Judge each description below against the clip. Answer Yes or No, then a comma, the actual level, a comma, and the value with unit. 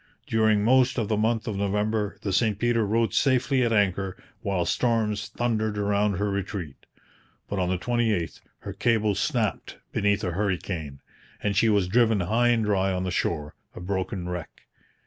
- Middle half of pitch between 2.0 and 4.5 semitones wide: Yes, average, 2.9 semitones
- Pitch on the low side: Yes, low, 105 Hz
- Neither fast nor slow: Yes, average, 170 wpm